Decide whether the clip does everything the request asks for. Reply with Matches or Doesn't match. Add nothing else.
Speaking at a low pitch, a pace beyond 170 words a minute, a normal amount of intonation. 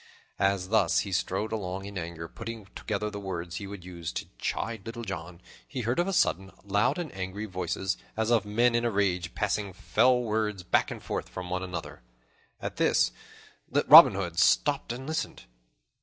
Matches